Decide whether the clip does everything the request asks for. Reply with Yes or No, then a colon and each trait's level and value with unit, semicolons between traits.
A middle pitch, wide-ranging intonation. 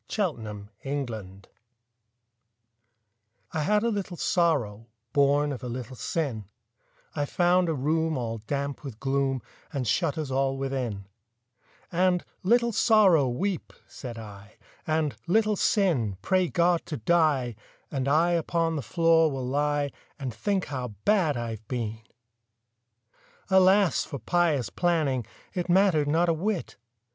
Yes: medium, 145 Hz; wide, 5.7 semitones